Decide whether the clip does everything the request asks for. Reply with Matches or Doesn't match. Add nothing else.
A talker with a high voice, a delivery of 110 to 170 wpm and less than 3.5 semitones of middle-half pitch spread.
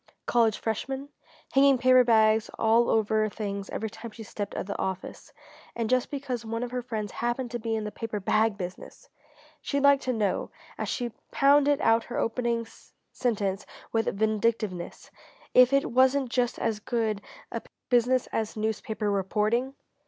Matches